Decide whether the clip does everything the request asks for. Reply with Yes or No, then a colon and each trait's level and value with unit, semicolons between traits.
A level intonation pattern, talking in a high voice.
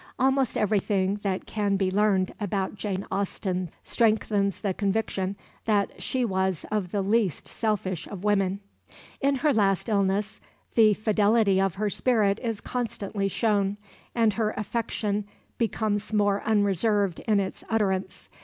Yes: narrow, 2.0 semitones; high, 205 Hz